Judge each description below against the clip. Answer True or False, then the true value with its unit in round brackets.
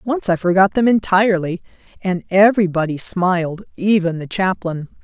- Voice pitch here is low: False (185 Hz)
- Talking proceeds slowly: True (120 wpm)